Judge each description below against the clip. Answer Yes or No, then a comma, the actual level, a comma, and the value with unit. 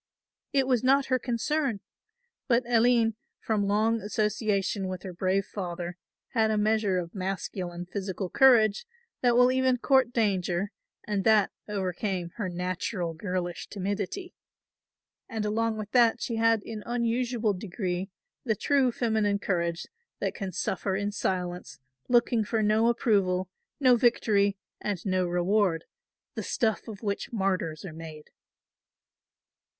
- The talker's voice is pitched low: No, high, 210 Hz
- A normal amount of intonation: Yes, average, 3.8 semitones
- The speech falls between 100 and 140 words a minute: Yes, slow, 135 wpm